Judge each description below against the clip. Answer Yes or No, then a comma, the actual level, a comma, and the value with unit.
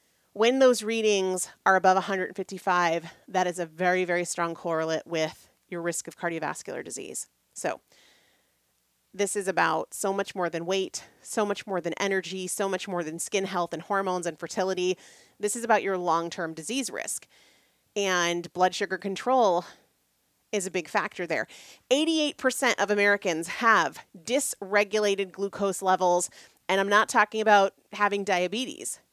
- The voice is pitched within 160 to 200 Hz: Yes, high, 190 Hz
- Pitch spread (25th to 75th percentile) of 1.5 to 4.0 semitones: Yes, average, 2.9 semitones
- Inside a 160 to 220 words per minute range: No, average, 150 wpm